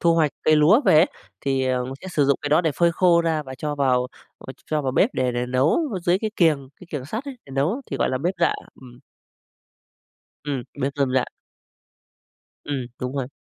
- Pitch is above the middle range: No, medium, 145 Hz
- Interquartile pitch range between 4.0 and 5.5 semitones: Yes, average, 4.3 semitones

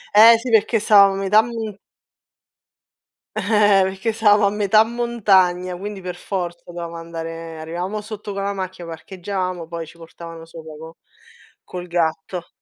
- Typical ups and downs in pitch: Yes, average, 3.7 semitones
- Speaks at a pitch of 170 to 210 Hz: Yes, medium, 185 Hz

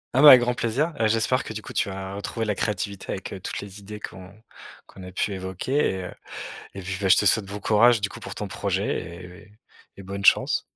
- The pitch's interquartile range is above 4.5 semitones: No, average, 2.8 semitones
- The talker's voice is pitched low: Yes, low, 100 Hz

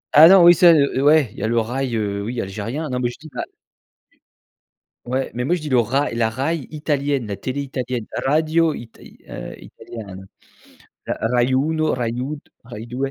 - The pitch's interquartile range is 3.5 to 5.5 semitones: Yes, average, 4.4 semitones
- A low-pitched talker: Yes, low, 130 Hz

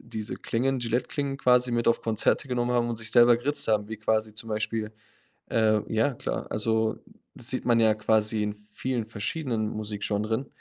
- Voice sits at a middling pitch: No, low, 115 Hz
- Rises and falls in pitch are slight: Yes, narrow, 2.0 semitones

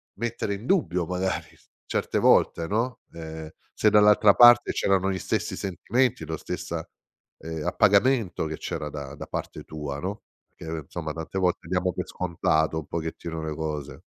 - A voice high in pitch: No, very low, 90 Hz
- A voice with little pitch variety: No, average, 4.5 semitones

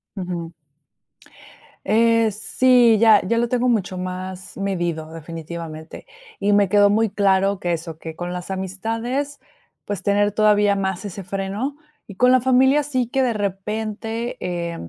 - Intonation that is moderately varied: Yes, average, 3.9 semitones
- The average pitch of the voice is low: No, high, 200 Hz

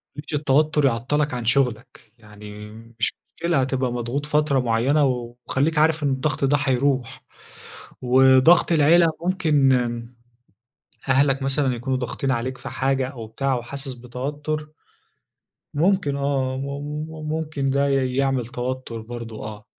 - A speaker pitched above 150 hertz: No, low, 135 Hz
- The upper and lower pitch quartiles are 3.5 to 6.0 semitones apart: No, average, 2.9 semitones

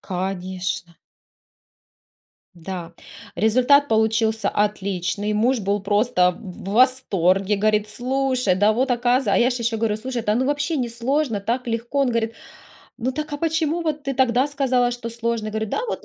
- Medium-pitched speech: No, high, 230 Hz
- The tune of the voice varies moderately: Yes, average, 3.9 semitones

